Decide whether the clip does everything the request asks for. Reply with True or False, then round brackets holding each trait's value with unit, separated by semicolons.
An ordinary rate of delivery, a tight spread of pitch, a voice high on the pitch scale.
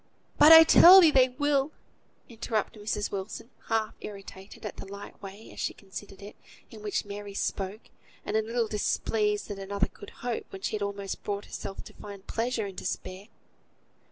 True (180 wpm; 2.3 semitones; 210 Hz)